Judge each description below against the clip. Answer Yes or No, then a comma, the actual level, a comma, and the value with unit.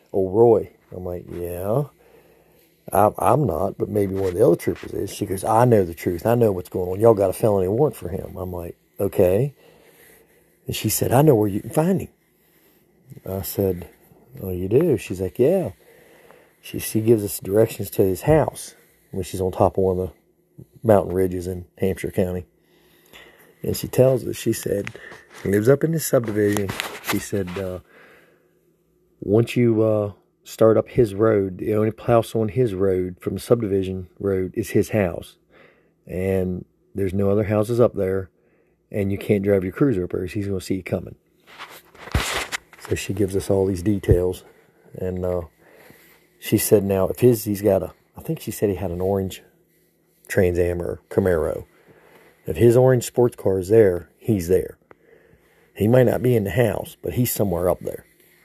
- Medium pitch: No, low, 100 Hz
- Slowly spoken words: No, average, 185 wpm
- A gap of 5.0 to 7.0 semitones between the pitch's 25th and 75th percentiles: No, average, 3.9 semitones